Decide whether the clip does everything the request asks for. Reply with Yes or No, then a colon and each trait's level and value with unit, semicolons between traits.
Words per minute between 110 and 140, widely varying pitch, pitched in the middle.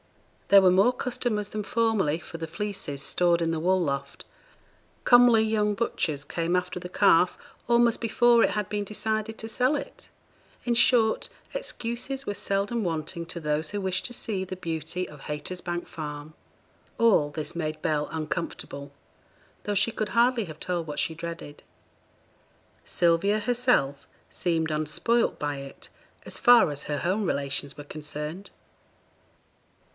No: average, 150 wpm; wide, 6.1 semitones; medium, 180 Hz